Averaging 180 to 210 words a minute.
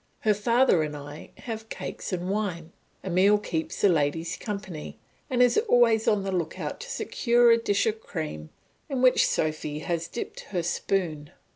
No: average, 170 wpm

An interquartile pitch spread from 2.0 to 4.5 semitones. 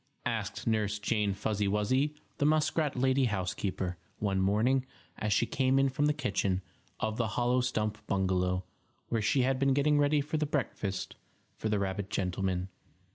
No: average, 5.2 semitones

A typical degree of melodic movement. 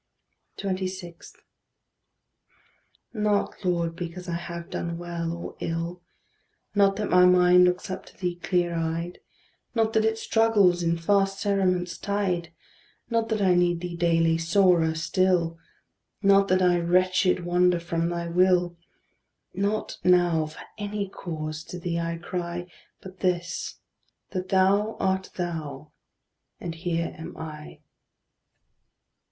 No: narrow, 2.0 semitones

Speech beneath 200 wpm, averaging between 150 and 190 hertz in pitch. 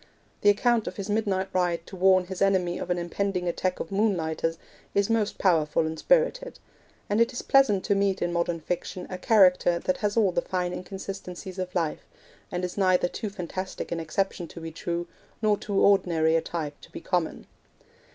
Yes: average, 190 wpm; medium, 185 Hz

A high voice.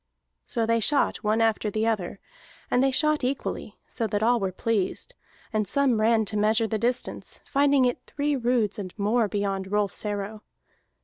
Yes: high, 220 Hz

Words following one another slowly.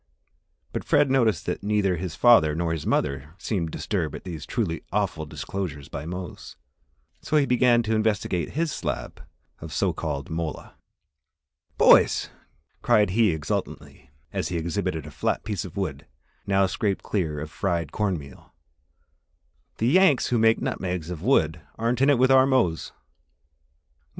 No: average, 150 wpm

